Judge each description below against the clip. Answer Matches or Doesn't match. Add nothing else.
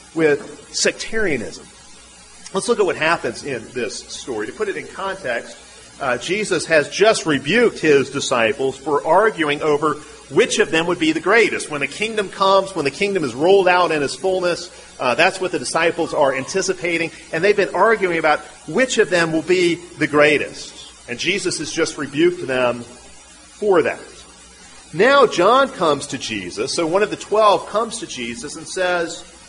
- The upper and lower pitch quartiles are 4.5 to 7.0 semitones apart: Matches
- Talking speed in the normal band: Matches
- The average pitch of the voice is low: Doesn't match